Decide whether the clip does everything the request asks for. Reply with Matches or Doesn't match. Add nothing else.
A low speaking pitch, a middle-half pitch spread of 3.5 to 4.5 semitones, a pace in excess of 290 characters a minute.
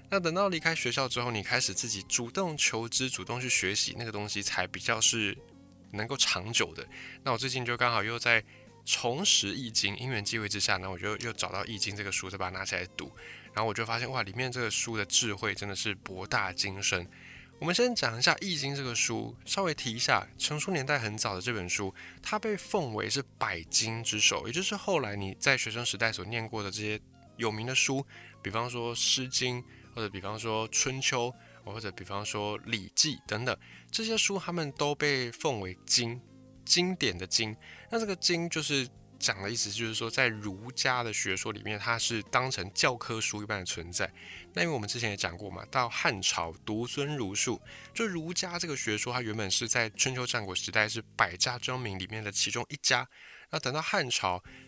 Matches